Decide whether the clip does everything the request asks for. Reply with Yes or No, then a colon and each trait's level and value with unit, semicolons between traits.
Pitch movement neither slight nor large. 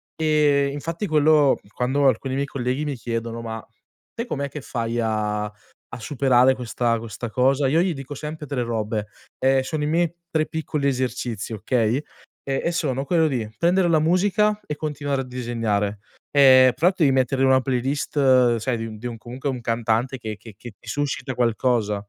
Yes: average, 4.1 semitones